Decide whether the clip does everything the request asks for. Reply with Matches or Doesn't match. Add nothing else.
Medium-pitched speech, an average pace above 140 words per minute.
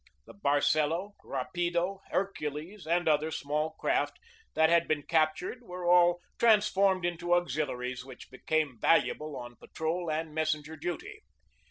Doesn't match